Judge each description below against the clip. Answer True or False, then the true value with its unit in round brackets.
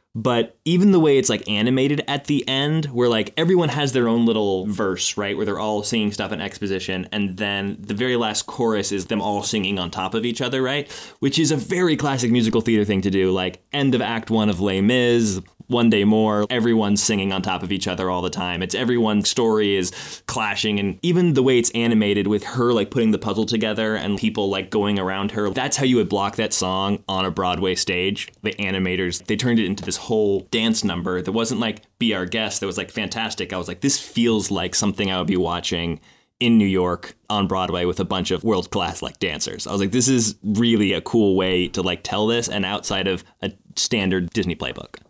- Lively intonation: False (3.6 semitones)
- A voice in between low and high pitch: False (105 Hz)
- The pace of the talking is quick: True (230 wpm)